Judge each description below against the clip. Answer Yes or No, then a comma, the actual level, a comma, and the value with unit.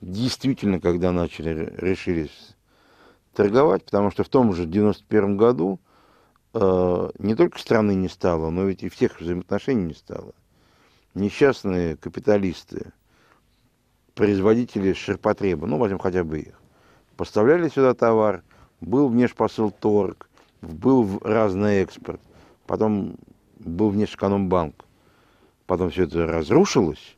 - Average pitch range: Yes, average, 3.3 semitones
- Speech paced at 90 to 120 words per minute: Yes, average, 115 wpm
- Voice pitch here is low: Yes, low, 100 Hz